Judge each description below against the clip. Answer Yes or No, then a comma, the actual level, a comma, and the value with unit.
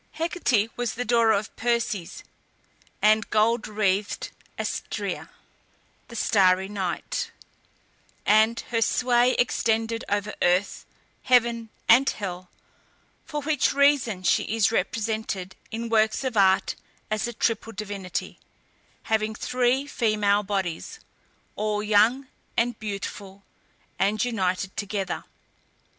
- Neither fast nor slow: No, slow, 110 wpm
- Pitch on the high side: Yes, high, 220 Hz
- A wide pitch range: No, average, 2.8 semitones